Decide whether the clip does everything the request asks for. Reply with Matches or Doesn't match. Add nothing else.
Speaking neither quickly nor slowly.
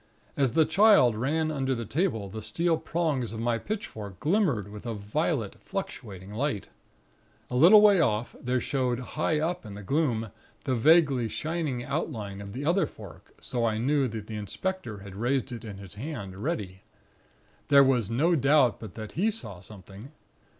Matches